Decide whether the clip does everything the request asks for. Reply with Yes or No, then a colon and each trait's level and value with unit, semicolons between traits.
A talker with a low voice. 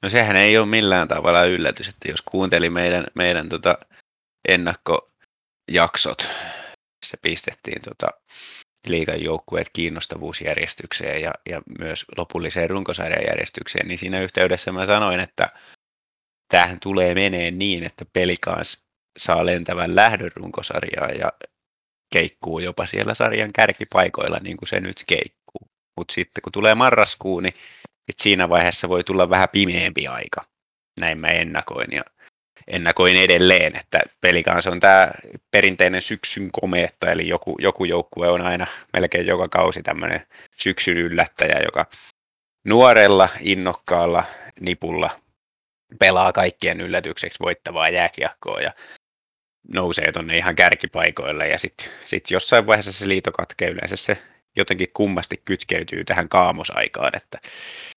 Yes: very low, 90 Hz